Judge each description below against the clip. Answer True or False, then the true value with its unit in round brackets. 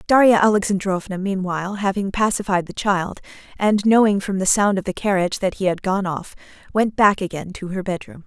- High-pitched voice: True (195 Hz)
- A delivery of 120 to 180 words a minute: False (190 wpm)